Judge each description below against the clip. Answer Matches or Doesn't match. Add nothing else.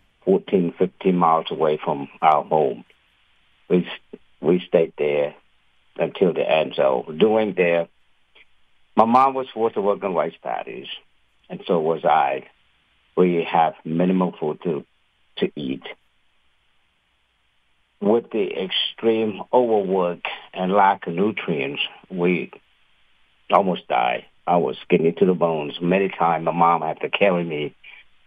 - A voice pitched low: Matches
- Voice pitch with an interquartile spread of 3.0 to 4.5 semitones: Matches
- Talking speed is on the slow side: Matches